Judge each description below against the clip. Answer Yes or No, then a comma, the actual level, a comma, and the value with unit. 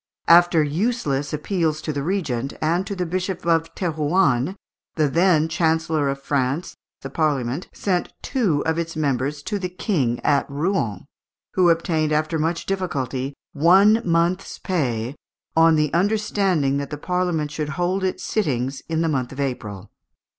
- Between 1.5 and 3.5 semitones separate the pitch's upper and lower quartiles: No, average, 4.2 semitones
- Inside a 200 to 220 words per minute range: No, average, 155 wpm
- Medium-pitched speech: Yes, medium, 160 Hz